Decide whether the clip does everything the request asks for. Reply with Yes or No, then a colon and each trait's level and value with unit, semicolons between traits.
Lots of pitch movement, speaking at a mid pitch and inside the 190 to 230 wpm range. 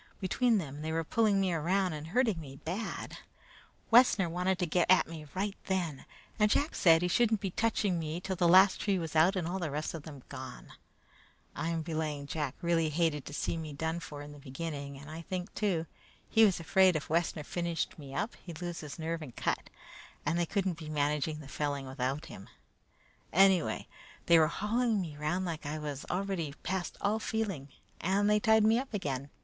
No: average, 4.1 semitones; medium, 165 Hz; average, 200 wpm